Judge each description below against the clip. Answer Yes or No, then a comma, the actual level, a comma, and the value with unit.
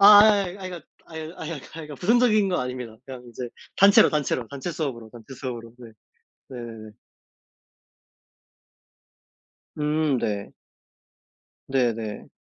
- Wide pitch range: Yes, wide, 6.8 semitones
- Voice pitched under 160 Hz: Yes, medium, 140 Hz